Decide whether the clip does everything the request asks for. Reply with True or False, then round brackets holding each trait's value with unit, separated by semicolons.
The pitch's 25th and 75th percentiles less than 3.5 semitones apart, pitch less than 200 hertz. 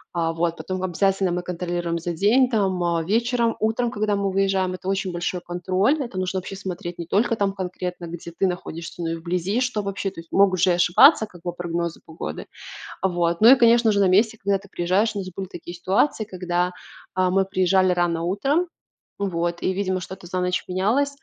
True (2.5 semitones; 185 Hz)